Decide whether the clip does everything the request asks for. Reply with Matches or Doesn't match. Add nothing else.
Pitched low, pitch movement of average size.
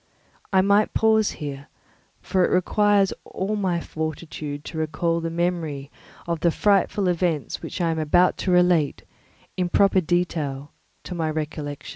Doesn't match